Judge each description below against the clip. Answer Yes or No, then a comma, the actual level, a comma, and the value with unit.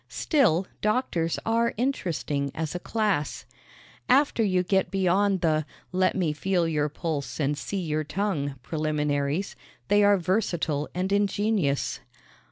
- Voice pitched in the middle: Yes, medium, 180 Hz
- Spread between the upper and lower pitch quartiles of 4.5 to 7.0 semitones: Yes, average, 5.0 semitones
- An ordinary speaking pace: No, slow, 130 wpm